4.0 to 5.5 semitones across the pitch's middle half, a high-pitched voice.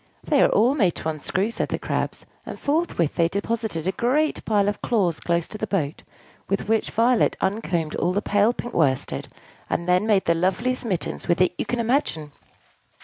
Yes: average, 5.2 semitones; high, 200 Hz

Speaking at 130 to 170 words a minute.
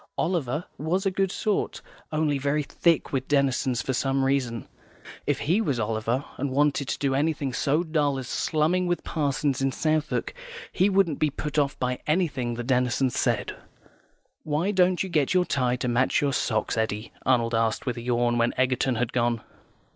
No: average, 180 wpm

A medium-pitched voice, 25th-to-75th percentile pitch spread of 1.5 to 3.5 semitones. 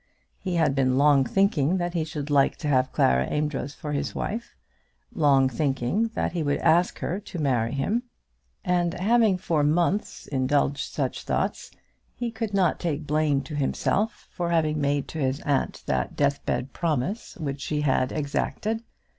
No: medium, 150 Hz; average, 4.2 semitones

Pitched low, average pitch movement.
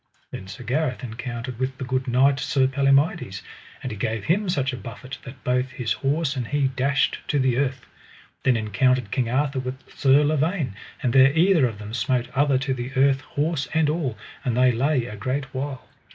No: low, 130 Hz; narrow, 2.2 semitones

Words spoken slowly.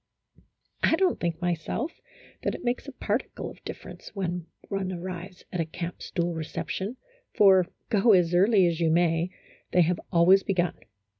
No: average, 165 wpm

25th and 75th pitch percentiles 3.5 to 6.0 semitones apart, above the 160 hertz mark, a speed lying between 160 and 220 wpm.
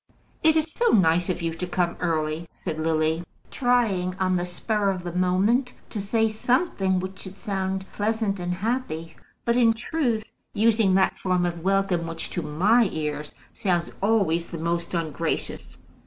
Yes: average, 4.4 semitones; medium, 185 Hz; average, 165 wpm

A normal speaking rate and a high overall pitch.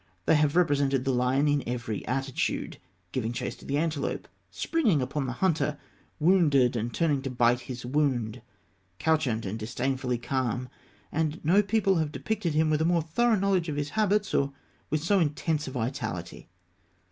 No: average, 170 wpm; medium, 145 Hz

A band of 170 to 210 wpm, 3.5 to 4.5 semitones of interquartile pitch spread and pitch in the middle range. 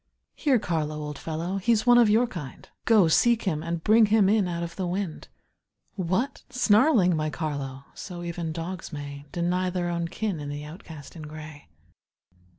No: average, 175 wpm; average, 5.0 semitones; medium, 175 Hz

